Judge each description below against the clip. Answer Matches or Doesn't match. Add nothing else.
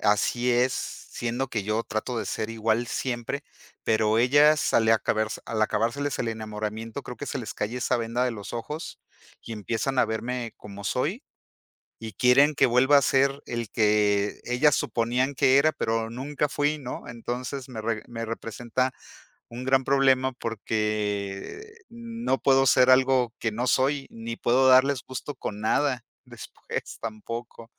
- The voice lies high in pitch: Doesn't match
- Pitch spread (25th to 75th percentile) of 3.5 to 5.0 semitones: Doesn't match